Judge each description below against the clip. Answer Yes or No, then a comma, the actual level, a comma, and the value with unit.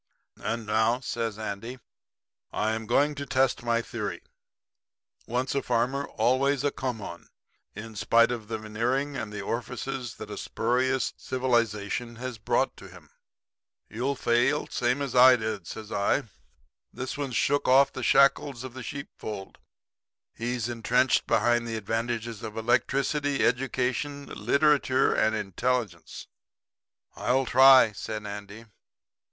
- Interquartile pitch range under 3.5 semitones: Yes, average, 2.9 semitones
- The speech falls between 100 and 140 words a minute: Yes, slow, 135 wpm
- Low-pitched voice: Yes, low, 120 Hz